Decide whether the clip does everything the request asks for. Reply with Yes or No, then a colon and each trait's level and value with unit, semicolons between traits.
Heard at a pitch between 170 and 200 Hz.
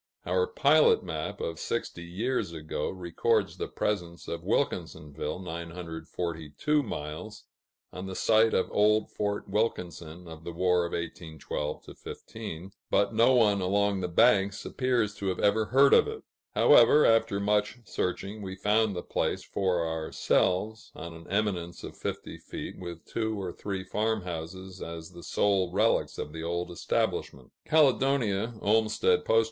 No: very low, 95 Hz